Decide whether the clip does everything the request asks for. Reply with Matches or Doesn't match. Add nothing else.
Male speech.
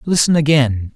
Matches